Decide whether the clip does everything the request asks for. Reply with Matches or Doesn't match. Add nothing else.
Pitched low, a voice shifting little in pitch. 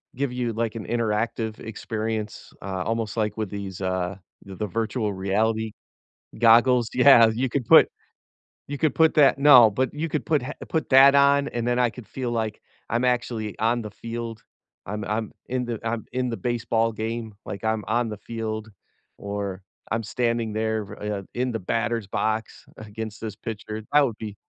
Matches